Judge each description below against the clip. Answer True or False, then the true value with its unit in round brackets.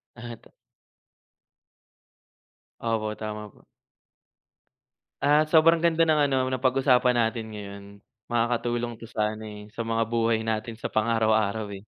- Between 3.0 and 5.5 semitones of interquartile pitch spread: False (2.4 semitones)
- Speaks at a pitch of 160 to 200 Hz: False (115 Hz)